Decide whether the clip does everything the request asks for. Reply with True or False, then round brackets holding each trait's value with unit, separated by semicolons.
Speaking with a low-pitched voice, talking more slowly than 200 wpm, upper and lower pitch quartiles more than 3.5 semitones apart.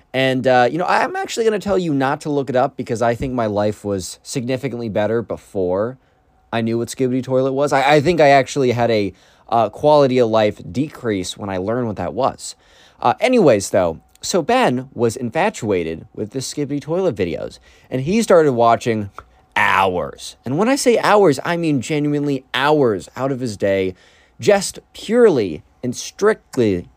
True (130 Hz; 180 wpm; 4.4 semitones)